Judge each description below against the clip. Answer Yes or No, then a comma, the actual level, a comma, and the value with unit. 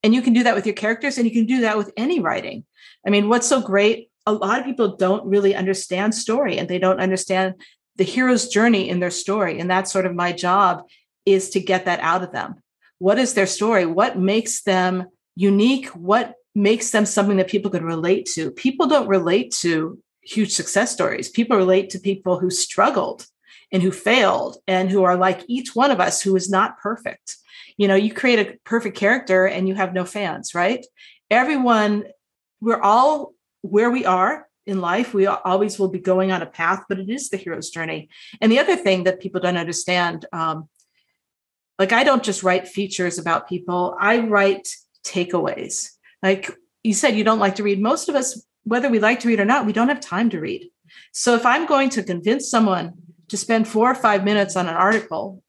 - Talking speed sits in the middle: No, fast, 210 wpm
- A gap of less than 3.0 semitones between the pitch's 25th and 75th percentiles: No, average, 3.7 semitones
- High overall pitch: Yes, high, 200 Hz